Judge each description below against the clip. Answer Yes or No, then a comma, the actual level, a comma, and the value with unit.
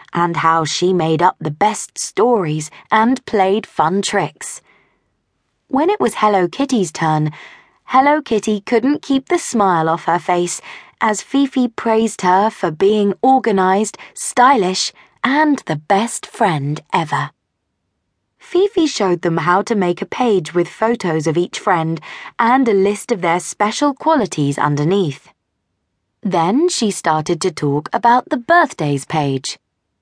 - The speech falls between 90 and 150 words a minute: Yes, average, 140 wpm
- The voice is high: Yes, high, 195 Hz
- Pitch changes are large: Yes, wide, 6.3 semitones